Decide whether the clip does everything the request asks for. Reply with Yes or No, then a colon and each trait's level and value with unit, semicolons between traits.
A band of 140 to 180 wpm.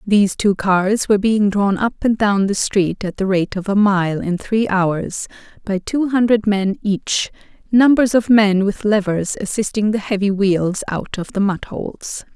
No: average, 190 wpm